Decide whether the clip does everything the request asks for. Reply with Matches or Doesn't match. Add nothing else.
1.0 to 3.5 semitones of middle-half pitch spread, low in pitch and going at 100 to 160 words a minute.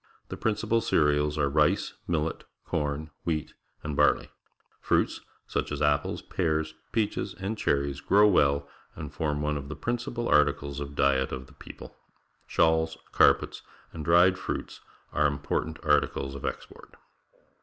Matches